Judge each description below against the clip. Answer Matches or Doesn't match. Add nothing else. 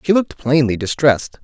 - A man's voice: Matches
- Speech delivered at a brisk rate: Doesn't match